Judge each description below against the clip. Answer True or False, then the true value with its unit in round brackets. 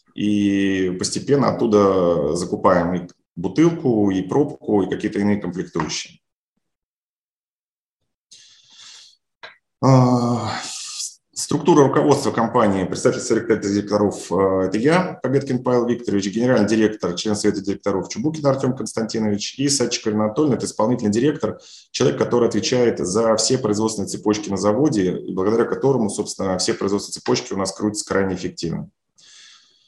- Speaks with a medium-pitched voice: False (105 Hz)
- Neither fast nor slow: True (120 wpm)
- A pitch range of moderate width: True (3.5 semitones)